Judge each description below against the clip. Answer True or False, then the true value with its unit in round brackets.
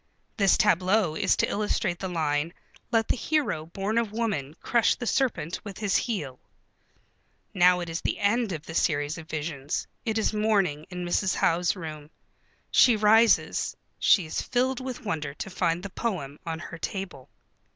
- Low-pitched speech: False (185 Hz)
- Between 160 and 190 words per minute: True (170 wpm)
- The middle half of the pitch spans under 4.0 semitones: False (5.4 semitones)